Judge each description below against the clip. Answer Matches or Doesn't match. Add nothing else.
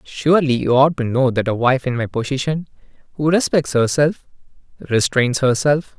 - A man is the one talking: Matches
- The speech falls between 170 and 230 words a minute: Doesn't match